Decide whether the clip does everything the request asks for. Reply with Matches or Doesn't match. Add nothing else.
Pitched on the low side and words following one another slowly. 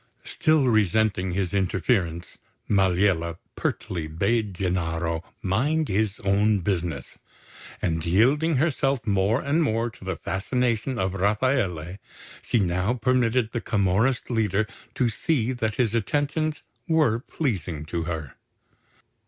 Matches